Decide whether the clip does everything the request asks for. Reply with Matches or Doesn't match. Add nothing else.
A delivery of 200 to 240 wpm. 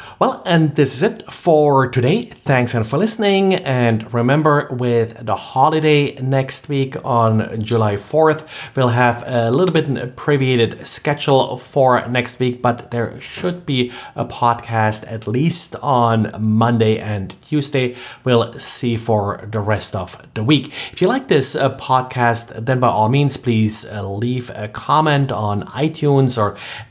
Doesn't match